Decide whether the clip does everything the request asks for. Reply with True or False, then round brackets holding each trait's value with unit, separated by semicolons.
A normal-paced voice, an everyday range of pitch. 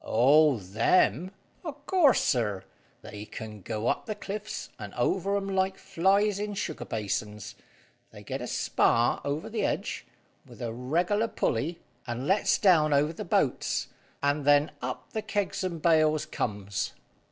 False (155 wpm; 8.7 semitones)